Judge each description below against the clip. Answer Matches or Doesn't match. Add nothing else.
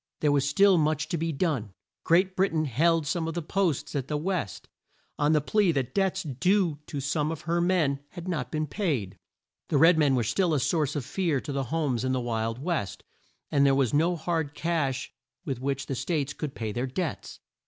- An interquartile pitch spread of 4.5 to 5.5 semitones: Doesn't match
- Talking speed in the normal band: Doesn't match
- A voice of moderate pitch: Matches